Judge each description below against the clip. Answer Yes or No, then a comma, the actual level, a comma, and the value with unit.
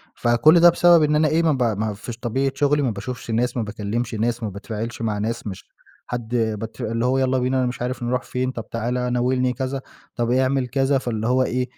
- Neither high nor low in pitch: No, low, 125 Hz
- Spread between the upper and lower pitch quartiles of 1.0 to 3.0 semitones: Yes, narrow, 2.4 semitones